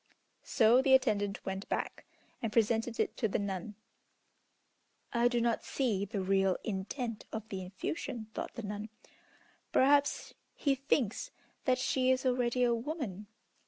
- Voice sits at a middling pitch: No, high, 230 Hz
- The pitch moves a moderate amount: Yes, average, 4.0 semitones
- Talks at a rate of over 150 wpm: No, average, 145 wpm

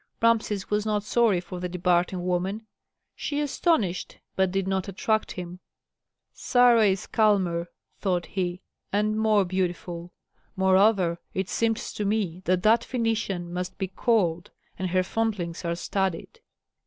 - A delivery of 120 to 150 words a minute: Yes, average, 140 wpm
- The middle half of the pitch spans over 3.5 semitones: No, average, 3.2 semitones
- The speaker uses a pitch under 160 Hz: No, high, 190 Hz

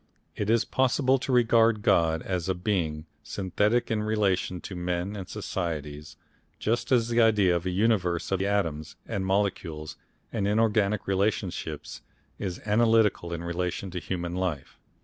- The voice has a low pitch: Yes, very low, 95 Hz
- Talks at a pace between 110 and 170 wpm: Yes, average, 150 wpm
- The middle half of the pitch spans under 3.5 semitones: No, average, 3.8 semitones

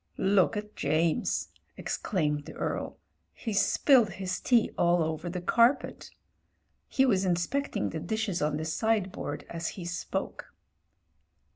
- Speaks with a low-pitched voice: No, medium, 185 Hz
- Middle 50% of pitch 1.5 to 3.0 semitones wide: No, average, 4.8 semitones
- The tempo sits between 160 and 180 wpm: No, average, 140 wpm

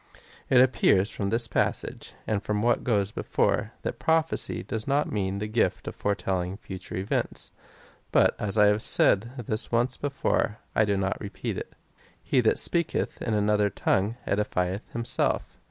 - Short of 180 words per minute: Yes, average, 165 wpm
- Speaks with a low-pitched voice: Yes, low, 105 Hz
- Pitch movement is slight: No, average, 3.0 semitones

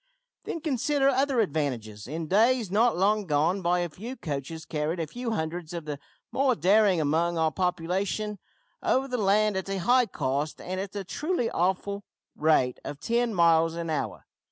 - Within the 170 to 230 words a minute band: Yes, average, 175 wpm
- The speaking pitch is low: No, medium, 185 Hz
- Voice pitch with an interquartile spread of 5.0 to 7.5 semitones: Yes, wide, 5.6 semitones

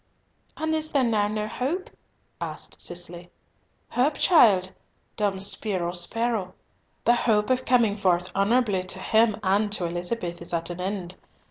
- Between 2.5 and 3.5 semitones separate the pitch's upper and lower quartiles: No, average, 4.5 semitones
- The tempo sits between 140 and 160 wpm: Yes, average, 145 wpm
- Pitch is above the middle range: Yes, high, 205 Hz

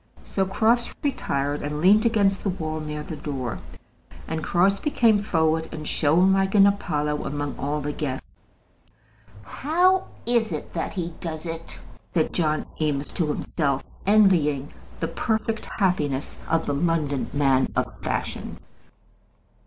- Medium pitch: Yes, medium, 160 Hz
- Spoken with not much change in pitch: No, average, 5.1 semitones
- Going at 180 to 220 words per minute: No, average, 140 wpm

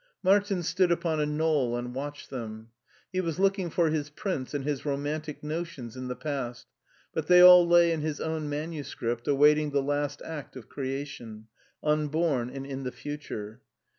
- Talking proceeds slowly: No, average, 170 wpm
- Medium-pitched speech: Yes, medium, 145 Hz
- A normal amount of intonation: Yes, average, 3.4 semitones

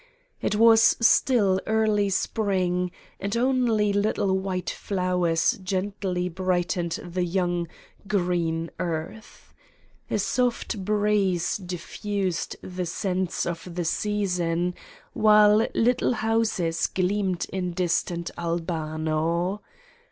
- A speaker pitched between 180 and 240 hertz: Yes, medium, 185 Hz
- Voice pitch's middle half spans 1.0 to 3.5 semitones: Yes, average, 3.0 semitones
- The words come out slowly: Yes, slow, 95 wpm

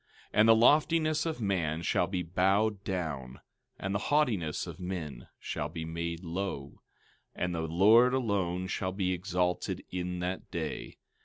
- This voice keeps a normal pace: Yes, average, 155 wpm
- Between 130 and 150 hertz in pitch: No, very low, 90 Hz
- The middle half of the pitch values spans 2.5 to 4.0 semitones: Yes, average, 3.4 semitones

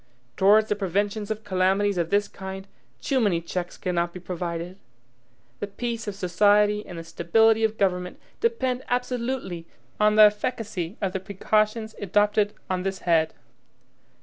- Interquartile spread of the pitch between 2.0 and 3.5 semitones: Yes, average, 3.1 semitones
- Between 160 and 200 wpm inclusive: No, average, 150 wpm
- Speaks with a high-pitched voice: Yes, high, 205 Hz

